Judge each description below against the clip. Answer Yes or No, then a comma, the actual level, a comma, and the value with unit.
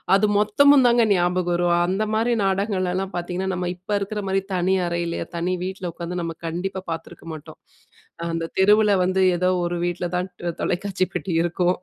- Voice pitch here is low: No, medium, 185 Hz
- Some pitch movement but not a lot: No, narrow, 1.9 semitones